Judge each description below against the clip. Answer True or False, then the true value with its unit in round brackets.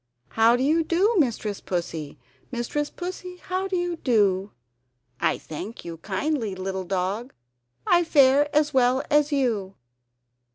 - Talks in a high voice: True (255 Hz)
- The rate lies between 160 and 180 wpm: False (135 wpm)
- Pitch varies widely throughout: True (7.8 semitones)